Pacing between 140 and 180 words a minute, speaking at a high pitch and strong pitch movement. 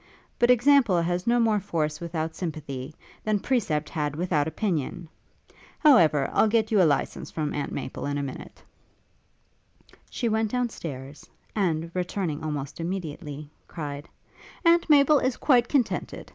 No: average, 145 wpm; medium, 170 Hz; wide, 6.9 semitones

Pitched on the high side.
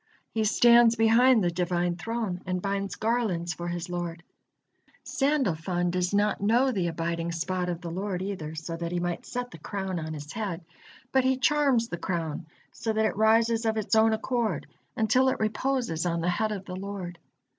Yes: high, 195 Hz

